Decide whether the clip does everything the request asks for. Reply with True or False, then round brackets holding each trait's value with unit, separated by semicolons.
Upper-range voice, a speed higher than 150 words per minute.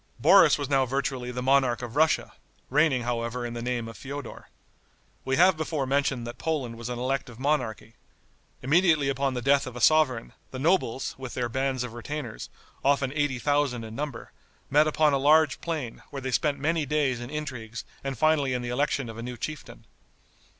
False (135 Hz; 190 wpm)